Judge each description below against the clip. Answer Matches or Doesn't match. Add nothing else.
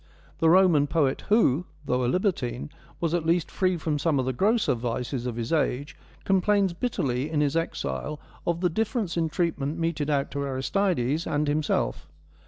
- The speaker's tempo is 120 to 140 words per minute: Doesn't match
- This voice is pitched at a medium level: Matches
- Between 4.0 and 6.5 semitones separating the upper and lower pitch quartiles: Matches